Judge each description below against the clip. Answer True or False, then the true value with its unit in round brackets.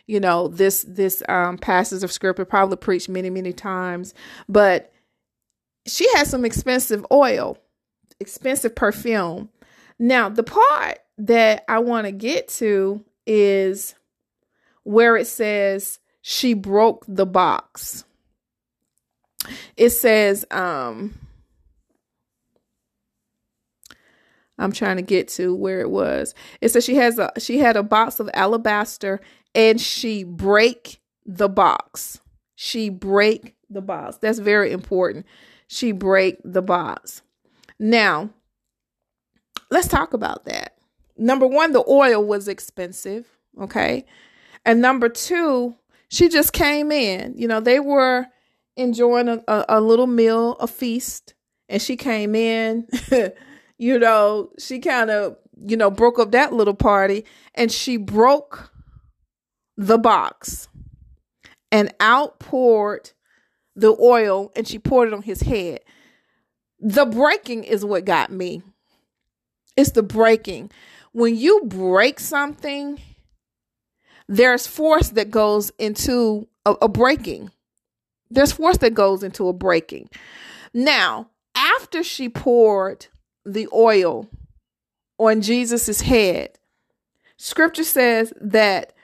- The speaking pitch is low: False (225 Hz)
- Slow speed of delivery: True (120 wpm)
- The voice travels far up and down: False (3.6 semitones)